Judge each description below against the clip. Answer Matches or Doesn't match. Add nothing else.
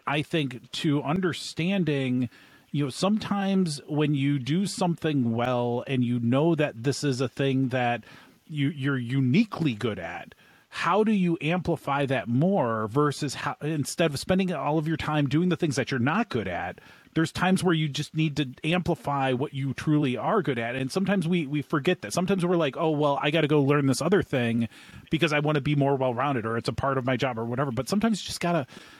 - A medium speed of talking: Doesn't match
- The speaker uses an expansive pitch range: Doesn't match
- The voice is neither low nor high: Matches